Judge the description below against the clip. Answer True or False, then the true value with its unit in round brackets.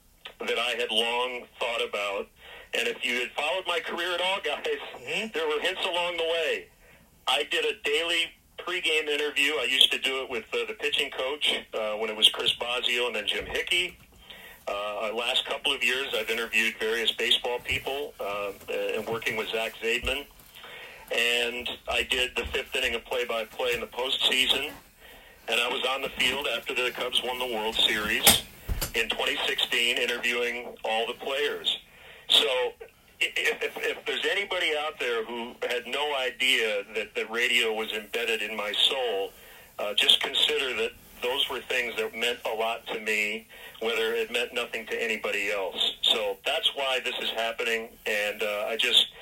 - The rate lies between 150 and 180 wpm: True (175 wpm)